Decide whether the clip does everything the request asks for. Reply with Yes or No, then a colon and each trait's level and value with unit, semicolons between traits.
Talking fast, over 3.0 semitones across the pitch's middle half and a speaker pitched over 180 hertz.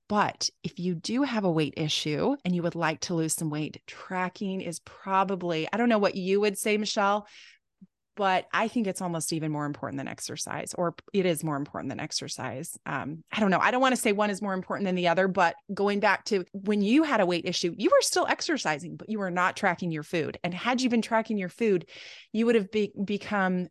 Yes: fast, 235 wpm; average, 3.8 semitones; high, 190 Hz